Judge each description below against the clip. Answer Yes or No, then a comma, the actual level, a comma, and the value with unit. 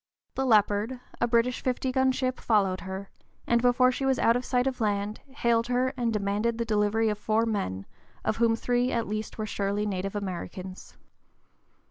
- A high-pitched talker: Yes, high, 225 Hz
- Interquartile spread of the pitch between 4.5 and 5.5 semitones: No, average, 3.2 semitones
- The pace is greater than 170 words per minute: Yes, average, 180 wpm